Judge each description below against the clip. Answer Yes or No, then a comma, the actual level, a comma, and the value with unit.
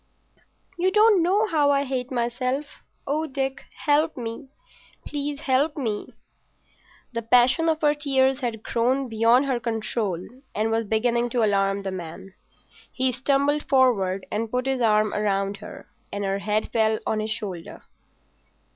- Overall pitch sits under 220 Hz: No, high, 245 Hz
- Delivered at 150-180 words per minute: No, average, 140 wpm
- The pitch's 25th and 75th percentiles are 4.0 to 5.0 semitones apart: Yes, average, 4.5 semitones